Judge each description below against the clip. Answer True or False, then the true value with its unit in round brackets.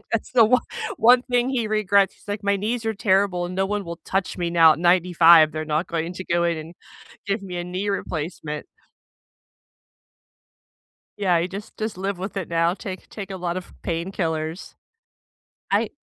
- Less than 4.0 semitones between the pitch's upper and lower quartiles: True (3.0 semitones)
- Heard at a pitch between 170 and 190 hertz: True (185 Hz)